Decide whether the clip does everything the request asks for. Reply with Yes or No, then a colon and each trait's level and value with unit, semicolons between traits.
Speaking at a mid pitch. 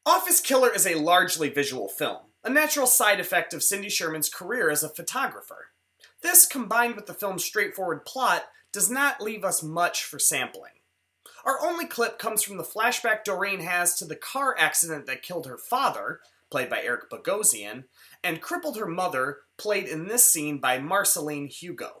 No: high, 195 Hz